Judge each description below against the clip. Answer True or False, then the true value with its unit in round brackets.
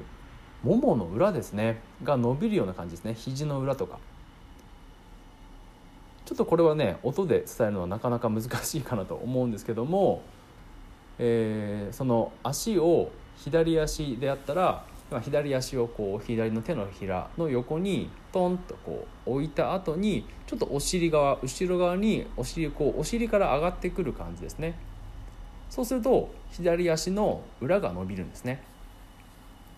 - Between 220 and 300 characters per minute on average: True (290 characters per minute)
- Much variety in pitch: True (8.7 semitones)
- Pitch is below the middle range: True (125 Hz)